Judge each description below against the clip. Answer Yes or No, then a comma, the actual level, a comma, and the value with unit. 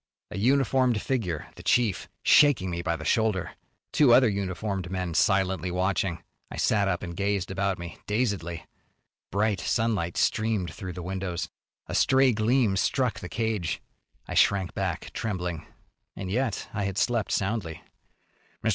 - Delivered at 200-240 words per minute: No, average, 150 wpm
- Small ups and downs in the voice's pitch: No, average, 3.8 semitones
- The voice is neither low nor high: No, low, 100 Hz